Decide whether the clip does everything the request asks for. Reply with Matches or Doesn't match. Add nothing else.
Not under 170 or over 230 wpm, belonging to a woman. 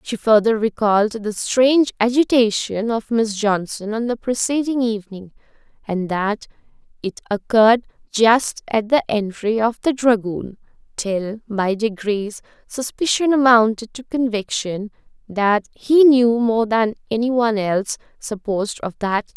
Doesn't match